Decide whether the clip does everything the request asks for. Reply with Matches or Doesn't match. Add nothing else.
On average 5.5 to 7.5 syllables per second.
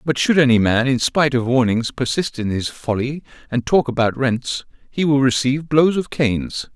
Doesn't match